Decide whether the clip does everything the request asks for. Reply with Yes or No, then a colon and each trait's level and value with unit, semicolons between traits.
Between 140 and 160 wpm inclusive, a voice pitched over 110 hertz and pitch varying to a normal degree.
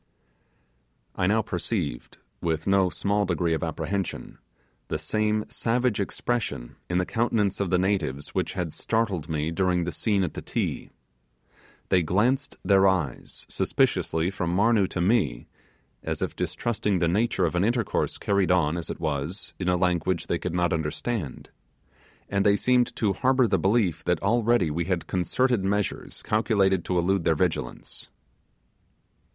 No: average, 155 wpm; very low, 95 Hz; average, 3.8 semitones